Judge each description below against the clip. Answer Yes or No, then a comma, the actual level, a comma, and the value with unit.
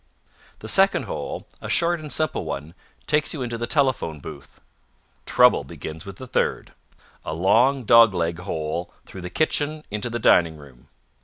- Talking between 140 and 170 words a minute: Yes, average, 165 wpm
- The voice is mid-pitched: No, low, 110 Hz